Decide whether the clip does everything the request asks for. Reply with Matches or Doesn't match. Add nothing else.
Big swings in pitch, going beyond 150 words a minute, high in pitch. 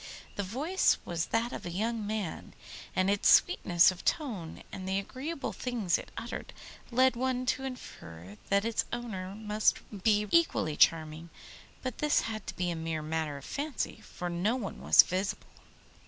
Matches